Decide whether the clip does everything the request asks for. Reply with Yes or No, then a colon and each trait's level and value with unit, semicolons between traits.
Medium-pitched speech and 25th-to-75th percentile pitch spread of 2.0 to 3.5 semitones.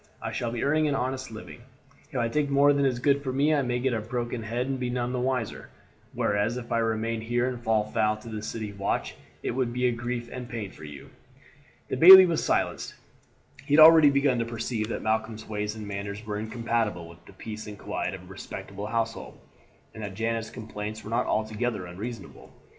No: low, 115 Hz; average, 2.8 semitones